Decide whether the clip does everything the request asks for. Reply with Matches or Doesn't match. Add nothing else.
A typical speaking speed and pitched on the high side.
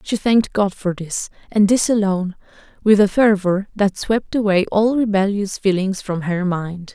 Matches